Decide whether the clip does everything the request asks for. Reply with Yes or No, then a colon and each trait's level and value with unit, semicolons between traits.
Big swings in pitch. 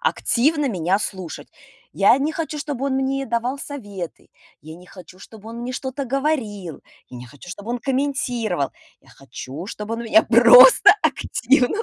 Yes: wide, 6.1 semitones